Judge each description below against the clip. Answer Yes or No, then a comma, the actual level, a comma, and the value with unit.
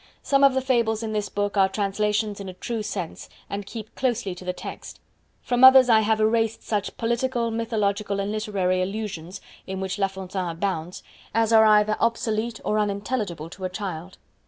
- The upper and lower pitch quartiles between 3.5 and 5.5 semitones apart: No, average, 2.8 semitones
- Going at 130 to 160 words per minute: No, average, 180 wpm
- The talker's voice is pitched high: Yes, high, 210 Hz